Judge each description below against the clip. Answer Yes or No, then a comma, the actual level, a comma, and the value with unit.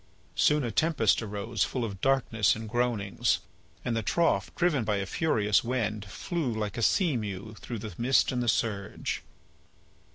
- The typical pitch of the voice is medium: No, low, 115 Hz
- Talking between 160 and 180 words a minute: Yes, average, 165 wpm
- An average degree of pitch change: Yes, average, 3.5 semitones